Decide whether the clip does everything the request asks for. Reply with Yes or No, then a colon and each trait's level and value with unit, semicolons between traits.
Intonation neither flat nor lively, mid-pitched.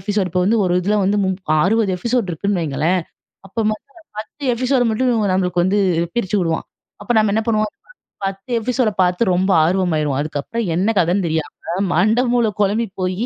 No: average, 3.7 semitones; high, 195 Hz